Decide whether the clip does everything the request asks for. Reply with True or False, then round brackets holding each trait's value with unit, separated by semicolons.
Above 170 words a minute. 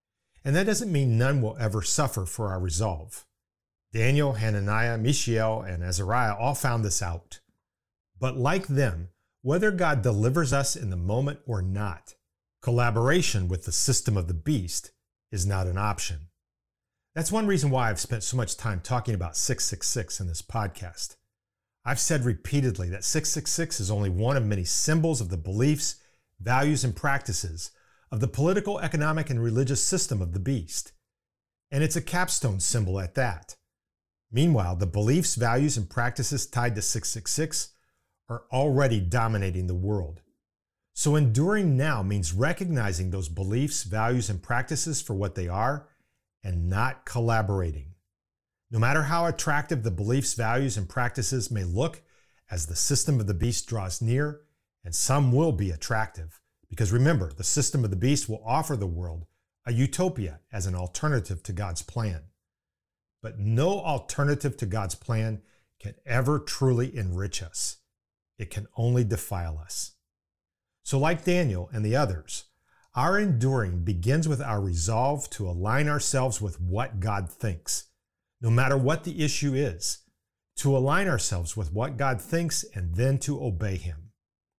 False (155 wpm)